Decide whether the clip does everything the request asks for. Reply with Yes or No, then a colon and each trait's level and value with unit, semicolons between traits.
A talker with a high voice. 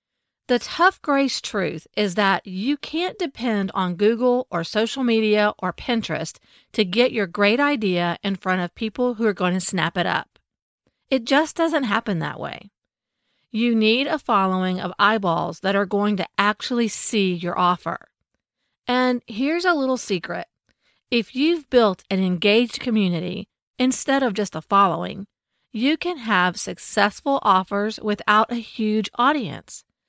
Yes: high, 215 Hz